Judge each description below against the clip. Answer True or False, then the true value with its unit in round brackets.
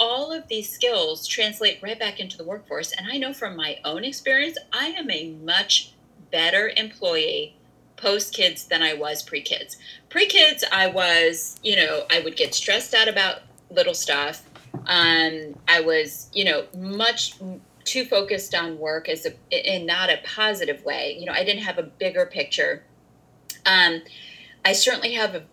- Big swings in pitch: True (8.6 semitones)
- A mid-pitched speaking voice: False (210 Hz)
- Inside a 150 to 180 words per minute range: True (165 wpm)